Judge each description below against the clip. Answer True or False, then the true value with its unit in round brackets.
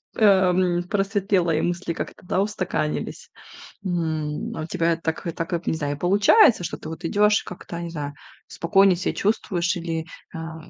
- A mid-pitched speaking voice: True (175 Hz)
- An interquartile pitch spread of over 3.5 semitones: False (2.9 semitones)